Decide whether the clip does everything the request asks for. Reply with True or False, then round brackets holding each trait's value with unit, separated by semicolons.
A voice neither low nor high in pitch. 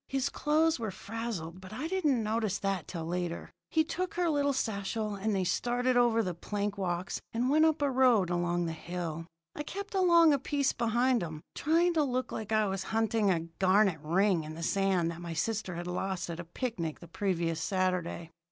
False (205 Hz)